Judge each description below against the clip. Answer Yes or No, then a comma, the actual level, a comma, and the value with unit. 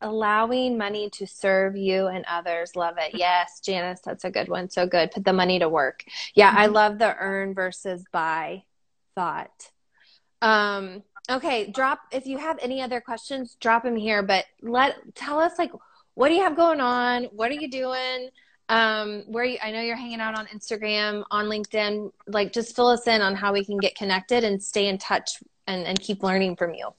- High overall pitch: Yes, high, 210 Hz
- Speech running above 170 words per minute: Yes, average, 200 wpm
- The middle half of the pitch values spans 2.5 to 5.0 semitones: Yes, average, 4.1 semitones